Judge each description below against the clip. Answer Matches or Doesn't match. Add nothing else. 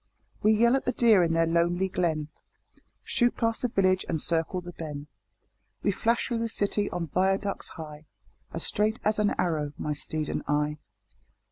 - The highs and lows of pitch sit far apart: Doesn't match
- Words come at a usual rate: Matches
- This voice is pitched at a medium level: Matches